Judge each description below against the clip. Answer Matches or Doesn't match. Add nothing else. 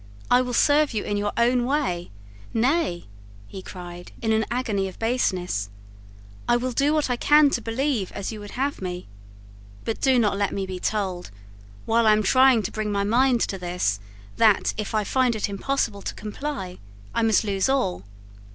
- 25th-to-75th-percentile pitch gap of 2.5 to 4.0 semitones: Doesn't match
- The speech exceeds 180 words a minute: Matches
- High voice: Matches